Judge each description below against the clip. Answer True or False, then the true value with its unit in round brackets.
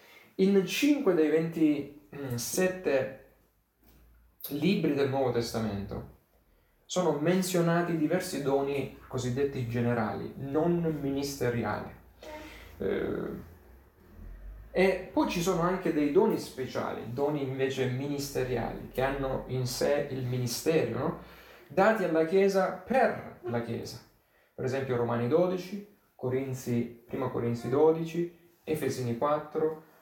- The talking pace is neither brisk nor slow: False (100 wpm)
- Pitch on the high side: False (140 Hz)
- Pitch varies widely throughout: True (5.9 semitones)